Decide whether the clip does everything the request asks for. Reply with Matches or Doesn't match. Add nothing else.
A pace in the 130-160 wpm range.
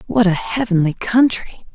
Matches